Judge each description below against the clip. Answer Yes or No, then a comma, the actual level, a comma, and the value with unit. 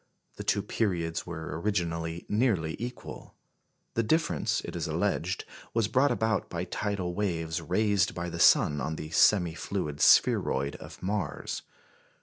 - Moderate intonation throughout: Yes, average, 4.3 semitones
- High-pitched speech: No, very low, 90 Hz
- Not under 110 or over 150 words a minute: Yes, average, 140 wpm